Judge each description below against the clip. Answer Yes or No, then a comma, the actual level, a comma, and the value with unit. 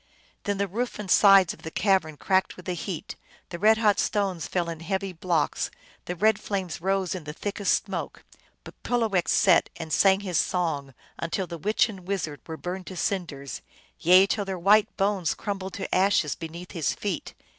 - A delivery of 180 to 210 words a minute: Yes, average, 190 wpm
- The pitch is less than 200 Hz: Yes, medium, 185 Hz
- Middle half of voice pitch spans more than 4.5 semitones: No, average, 2.9 semitones